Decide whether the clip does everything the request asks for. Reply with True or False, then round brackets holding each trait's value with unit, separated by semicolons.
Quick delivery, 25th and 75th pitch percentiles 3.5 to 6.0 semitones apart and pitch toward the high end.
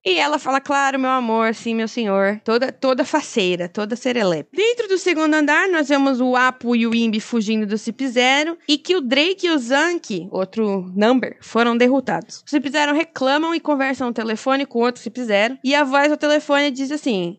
True (205 wpm; 4.6 semitones; 260 Hz)